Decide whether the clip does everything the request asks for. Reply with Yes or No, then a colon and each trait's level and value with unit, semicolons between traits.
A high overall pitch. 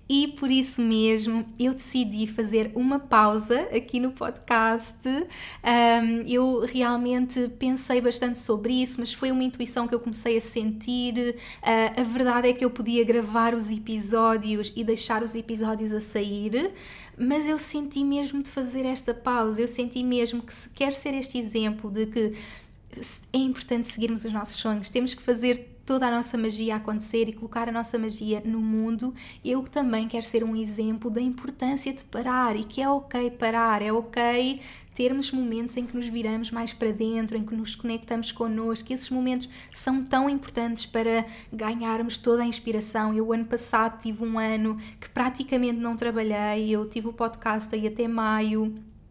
Yes: high, 235 Hz